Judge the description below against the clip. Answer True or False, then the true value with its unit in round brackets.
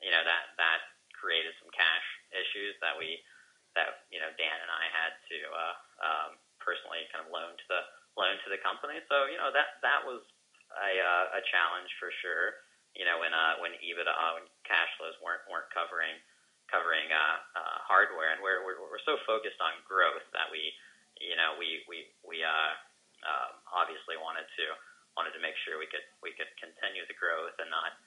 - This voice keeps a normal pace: True (195 wpm)